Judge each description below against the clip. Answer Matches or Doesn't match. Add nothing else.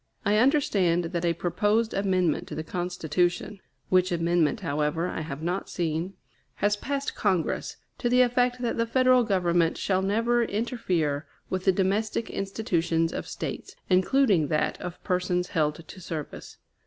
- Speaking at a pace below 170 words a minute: Matches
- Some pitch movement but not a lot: Matches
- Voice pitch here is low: Doesn't match